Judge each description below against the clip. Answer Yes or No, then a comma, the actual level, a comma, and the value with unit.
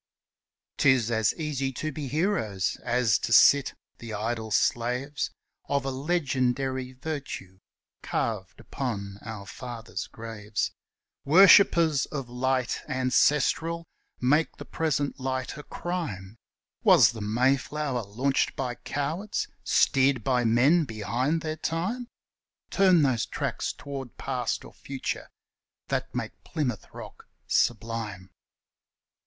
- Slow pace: Yes, slow, 115 wpm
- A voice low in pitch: Yes, low, 130 Hz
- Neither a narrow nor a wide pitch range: Yes, average, 4.4 semitones